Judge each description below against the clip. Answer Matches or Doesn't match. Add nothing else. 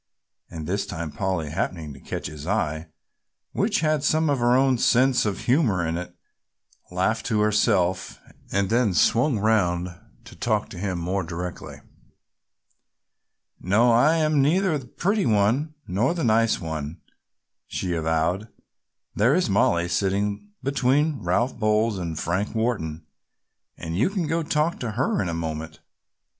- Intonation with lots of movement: Matches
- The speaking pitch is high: Doesn't match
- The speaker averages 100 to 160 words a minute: Matches